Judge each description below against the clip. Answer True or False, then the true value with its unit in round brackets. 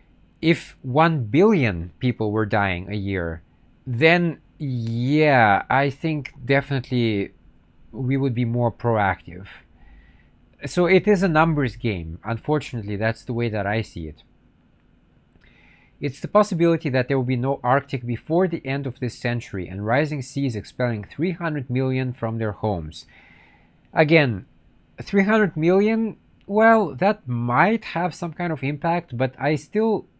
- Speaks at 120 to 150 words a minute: True (140 wpm)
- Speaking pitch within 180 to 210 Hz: False (125 Hz)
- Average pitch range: False (7.9 semitones)